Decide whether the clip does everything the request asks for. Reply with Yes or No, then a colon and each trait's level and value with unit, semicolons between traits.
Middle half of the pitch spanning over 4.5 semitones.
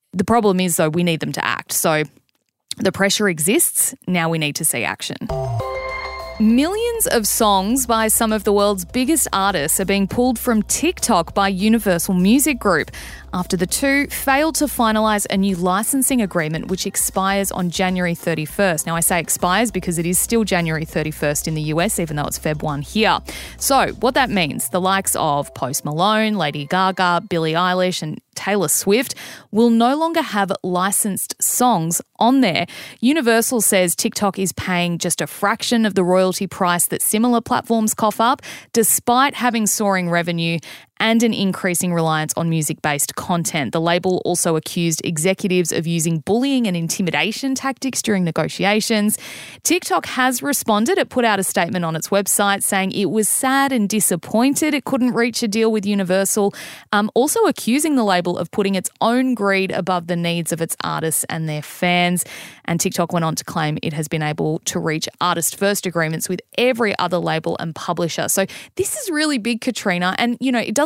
Yes: average, 5.0 semitones